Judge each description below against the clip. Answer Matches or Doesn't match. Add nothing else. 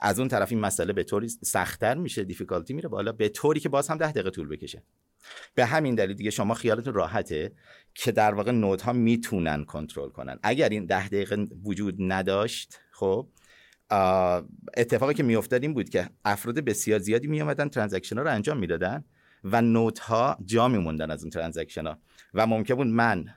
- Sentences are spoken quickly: Matches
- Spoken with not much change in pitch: Doesn't match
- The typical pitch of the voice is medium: Doesn't match